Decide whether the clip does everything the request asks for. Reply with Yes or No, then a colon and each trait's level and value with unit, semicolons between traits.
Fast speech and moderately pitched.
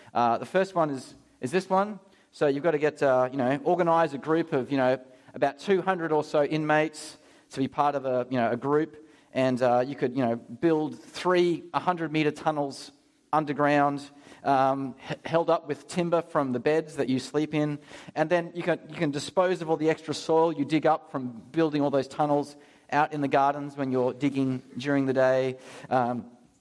Yes: fast, 215 wpm; medium, 145 Hz